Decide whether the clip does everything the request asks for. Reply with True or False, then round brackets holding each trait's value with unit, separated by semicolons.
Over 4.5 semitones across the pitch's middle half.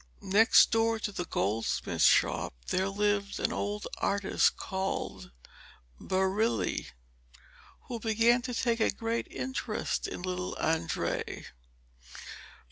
False (3.2 semitones)